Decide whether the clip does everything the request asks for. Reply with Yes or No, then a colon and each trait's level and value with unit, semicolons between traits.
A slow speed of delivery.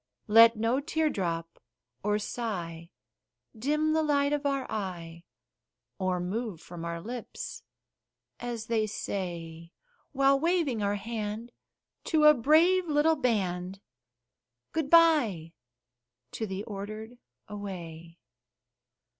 Yes: slow, 110 wpm